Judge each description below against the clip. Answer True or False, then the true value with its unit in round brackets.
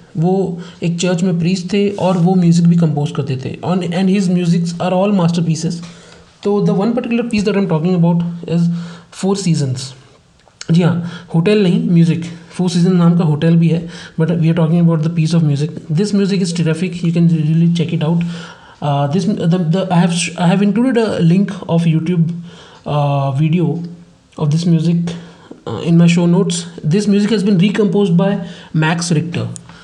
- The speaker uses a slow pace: False (170 wpm)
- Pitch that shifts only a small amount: True (2.1 semitones)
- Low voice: False (170 Hz)